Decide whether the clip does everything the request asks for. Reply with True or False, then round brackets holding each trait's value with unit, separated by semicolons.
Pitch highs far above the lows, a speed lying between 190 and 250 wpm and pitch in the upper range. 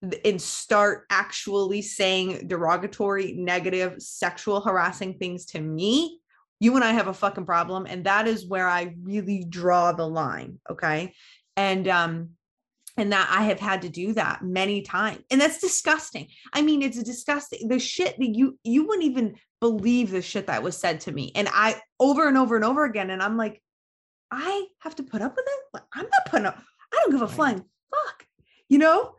True (6.2 semitones; 195 wpm; 210 Hz)